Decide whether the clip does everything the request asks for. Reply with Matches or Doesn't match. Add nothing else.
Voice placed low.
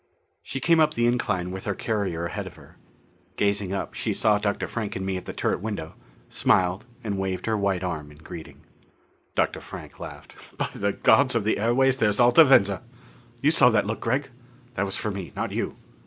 Matches